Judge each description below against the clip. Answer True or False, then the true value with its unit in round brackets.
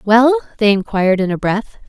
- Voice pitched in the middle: False (220 Hz)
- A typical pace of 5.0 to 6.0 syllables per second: True (5.2 syllables/s)